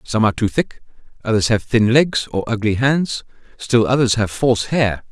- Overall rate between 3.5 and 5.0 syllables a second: Yes, 4.9 syllables/s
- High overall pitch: No, low, 115 Hz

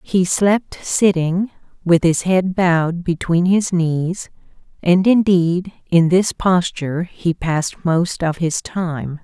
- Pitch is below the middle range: No, medium, 175 Hz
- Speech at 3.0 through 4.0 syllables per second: Yes, 3.4 syllables/s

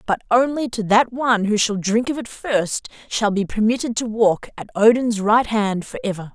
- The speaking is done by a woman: Yes, female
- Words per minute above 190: Yes, average, 200 wpm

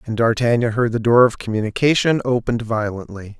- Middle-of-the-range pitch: No, low, 115 Hz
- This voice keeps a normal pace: Yes, average, 160 wpm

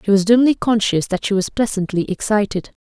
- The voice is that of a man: No, female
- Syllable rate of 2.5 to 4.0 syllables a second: No, 5.7 syllables/s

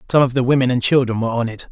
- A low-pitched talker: Yes, low, 125 Hz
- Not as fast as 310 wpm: No, fast, 315 wpm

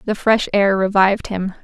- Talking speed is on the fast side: No, average, 185 wpm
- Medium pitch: No, high, 200 Hz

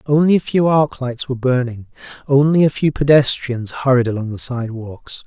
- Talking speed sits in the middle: Yes, average, 180 wpm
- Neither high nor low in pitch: No, low, 130 Hz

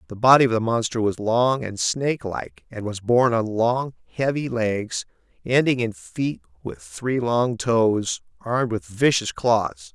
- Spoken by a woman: No, male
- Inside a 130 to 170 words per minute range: Yes, average, 165 wpm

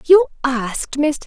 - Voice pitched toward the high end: Yes, very high, 285 Hz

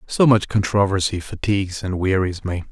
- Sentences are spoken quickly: No, average, 155 wpm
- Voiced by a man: Yes, male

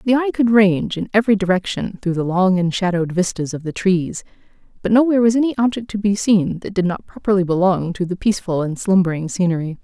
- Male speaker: No, female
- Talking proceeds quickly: Yes, fast, 215 wpm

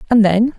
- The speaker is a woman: Yes, female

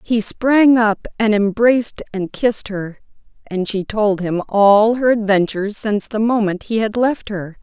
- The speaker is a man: No, female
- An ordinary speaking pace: Yes, average, 175 wpm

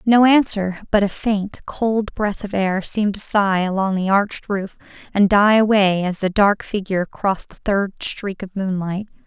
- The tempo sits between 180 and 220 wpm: Yes, average, 190 wpm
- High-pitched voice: Yes, high, 200 Hz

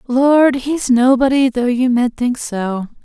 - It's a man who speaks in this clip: No, female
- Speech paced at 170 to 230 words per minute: No, average, 160 wpm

